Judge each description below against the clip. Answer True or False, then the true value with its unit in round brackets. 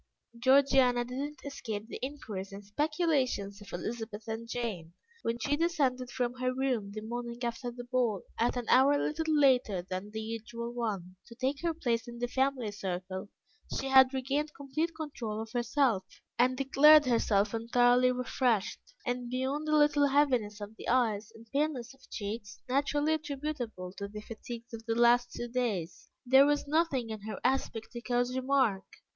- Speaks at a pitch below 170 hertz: False (245 Hz)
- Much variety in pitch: False (3.5 semitones)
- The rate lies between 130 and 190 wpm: True (170 wpm)